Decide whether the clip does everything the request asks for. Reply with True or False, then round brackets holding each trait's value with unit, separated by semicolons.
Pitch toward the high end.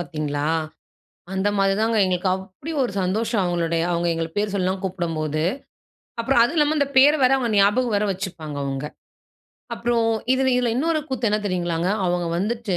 True (195 Hz)